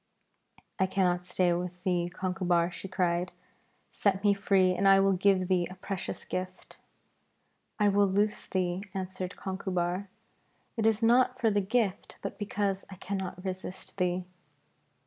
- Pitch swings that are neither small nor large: No, narrow, 1.7 semitones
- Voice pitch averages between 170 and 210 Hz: Yes, high, 190 Hz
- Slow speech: No, average, 145 wpm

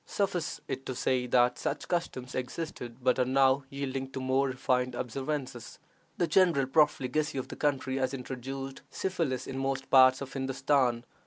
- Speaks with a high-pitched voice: No, low, 135 Hz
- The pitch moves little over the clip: Yes, narrow, 1.4 semitones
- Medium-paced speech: Yes, average, 160 wpm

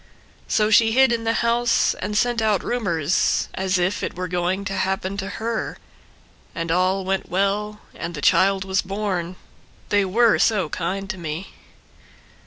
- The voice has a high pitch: Yes, high, 195 Hz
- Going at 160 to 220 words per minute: Yes, average, 165 wpm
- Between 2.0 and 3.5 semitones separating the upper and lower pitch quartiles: Yes, narrow, 2.6 semitones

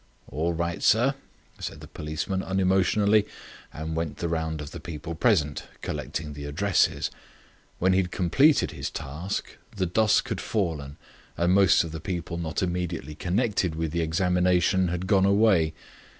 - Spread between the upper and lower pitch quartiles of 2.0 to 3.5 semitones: Yes, average, 3.1 semitones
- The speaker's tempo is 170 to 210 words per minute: No, average, 155 wpm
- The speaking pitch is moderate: No, very low, 85 Hz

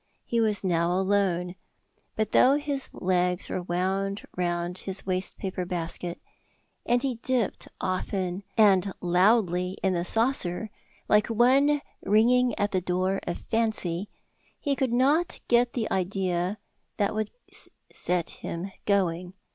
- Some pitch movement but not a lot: Yes, average, 4.1 semitones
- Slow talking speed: Yes, slow, 130 wpm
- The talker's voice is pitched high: Yes, high, 195 Hz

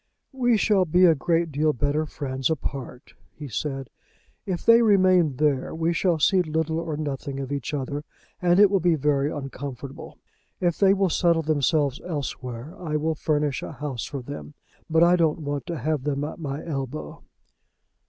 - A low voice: No, medium, 155 Hz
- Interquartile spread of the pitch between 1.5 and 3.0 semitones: No, average, 3.4 semitones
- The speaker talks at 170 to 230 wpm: Yes, average, 175 wpm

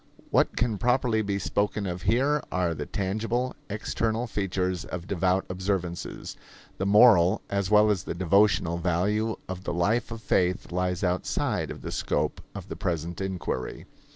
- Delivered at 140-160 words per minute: Yes, average, 155 wpm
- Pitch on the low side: Yes, very low, 95 Hz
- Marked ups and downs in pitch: No, average, 3.2 semitones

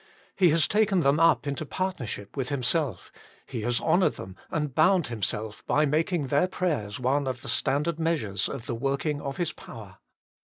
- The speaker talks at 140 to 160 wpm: No, average, 180 wpm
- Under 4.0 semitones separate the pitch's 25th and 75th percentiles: No, average, 5.3 semitones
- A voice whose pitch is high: No, medium, 140 Hz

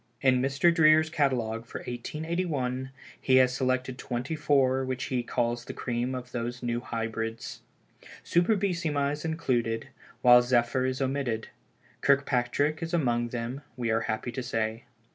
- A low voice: Yes, low, 130 Hz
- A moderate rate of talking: Yes, average, 145 wpm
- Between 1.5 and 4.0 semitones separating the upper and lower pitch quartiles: Yes, average, 3.1 semitones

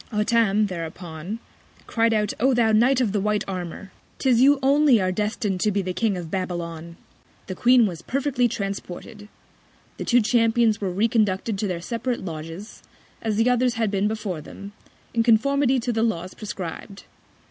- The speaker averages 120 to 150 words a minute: No, average, 170 wpm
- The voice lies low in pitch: No, high, 210 Hz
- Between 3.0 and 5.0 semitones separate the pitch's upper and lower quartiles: Yes, average, 3.9 semitones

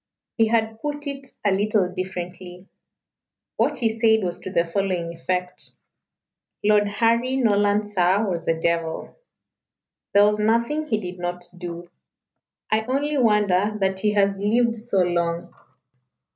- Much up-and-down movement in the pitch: No, average, 3.7 semitones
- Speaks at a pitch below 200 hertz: No, high, 205 Hz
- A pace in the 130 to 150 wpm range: Yes, average, 140 wpm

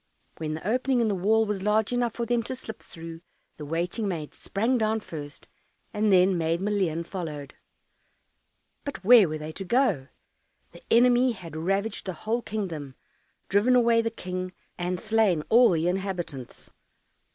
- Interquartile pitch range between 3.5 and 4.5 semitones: No, average, 5.2 semitones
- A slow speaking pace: No, average, 165 wpm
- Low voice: No, high, 195 Hz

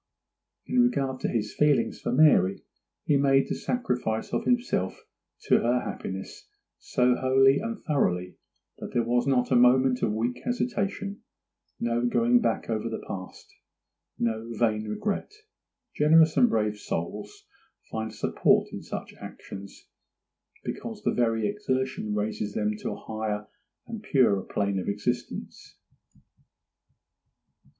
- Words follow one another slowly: Yes, slow, 130 wpm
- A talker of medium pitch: No, low, 120 Hz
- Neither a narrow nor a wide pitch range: Yes, average, 4.8 semitones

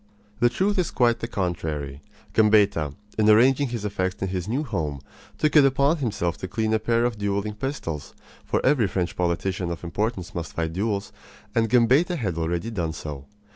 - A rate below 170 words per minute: No, average, 180 wpm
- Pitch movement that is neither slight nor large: No, wide, 5.8 semitones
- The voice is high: No, low, 105 Hz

